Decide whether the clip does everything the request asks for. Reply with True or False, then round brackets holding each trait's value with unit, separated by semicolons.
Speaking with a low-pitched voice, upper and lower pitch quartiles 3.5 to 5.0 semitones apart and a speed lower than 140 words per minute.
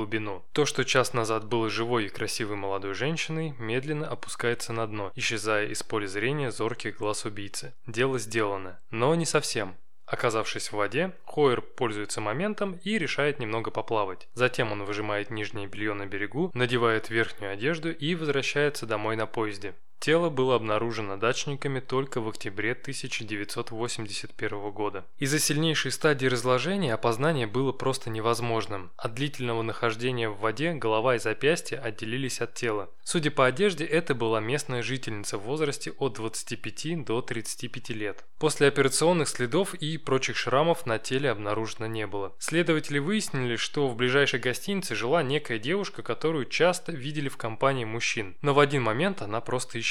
False (125 Hz; 4.7 semitones; 155 wpm)